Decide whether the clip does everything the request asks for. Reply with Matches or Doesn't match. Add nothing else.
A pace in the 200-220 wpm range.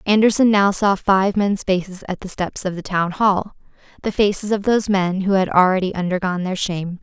Matches